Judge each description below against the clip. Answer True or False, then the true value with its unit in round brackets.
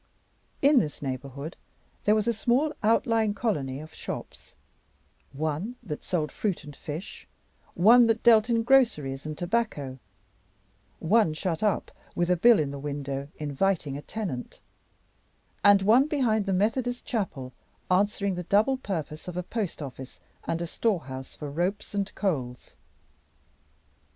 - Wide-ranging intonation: True (7.1 semitones)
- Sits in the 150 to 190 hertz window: True (185 Hz)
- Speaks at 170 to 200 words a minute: False (140 wpm)